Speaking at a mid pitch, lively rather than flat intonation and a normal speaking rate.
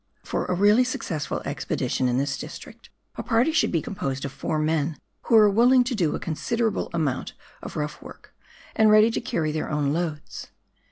Yes: medium, 170 Hz; wide, 7.0 semitones; average, 190 wpm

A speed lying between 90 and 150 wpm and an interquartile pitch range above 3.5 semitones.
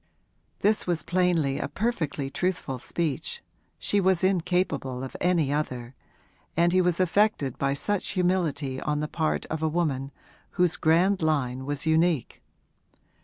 Yes: average, 140 wpm; average, 4.5 semitones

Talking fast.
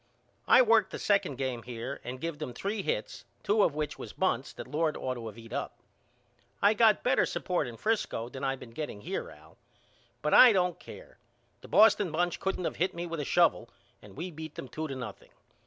Yes: fast, 215 wpm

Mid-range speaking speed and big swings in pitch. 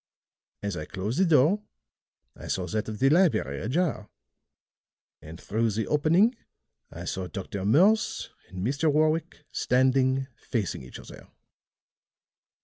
No: slow, 130 wpm; wide, 7.6 semitones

